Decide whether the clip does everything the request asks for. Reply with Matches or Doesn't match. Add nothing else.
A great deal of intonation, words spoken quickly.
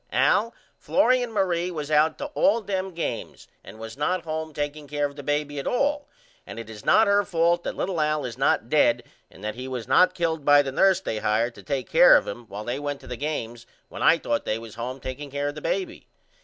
Matches